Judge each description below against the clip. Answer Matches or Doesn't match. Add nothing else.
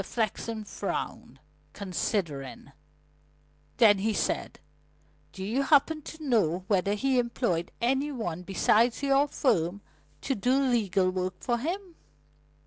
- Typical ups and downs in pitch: Doesn't match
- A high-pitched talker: Matches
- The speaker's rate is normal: Doesn't match